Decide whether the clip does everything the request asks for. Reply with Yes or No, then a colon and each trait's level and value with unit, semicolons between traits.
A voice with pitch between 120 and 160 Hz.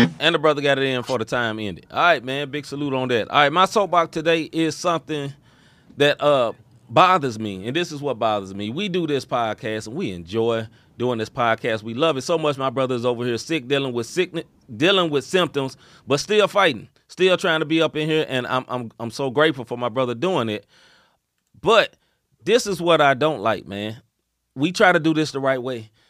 Yes: medium, 140 Hz